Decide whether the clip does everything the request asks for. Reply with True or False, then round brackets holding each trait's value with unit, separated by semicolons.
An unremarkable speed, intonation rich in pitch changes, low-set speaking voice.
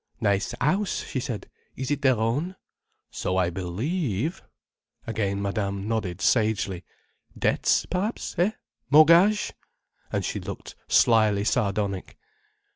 False (110 wpm; 7.4 semitones; 110 Hz)